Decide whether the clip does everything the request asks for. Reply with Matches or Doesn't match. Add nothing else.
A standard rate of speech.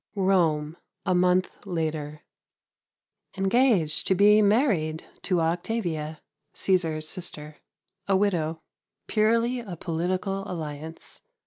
Doesn't match